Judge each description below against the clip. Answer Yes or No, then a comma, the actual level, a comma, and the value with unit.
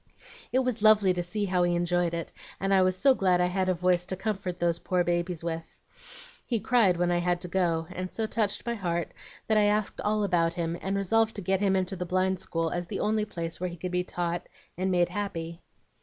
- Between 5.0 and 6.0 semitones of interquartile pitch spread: No, narrow, 2.5 semitones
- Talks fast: Yes, fast, 235 wpm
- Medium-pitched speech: Yes, medium, 180 Hz